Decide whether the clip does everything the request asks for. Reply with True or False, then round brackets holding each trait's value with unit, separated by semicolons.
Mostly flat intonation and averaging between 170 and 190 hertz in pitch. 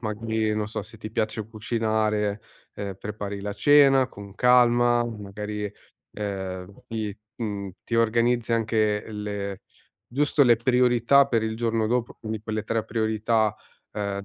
False (2.2 semitones; 110 Hz)